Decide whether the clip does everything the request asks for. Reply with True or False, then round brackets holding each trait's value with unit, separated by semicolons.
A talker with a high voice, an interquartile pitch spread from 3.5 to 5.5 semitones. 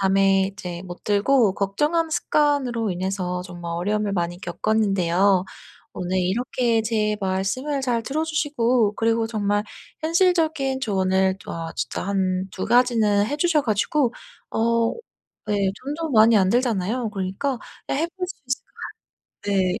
True (215 Hz; 5.1 semitones)